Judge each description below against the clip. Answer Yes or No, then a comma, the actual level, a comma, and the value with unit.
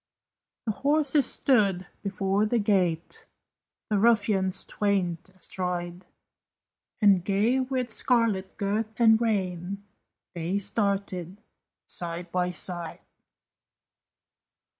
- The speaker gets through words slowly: Yes, slow, 90 wpm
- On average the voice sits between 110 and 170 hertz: No, high, 200 Hz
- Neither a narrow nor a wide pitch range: Yes, average, 3.7 semitones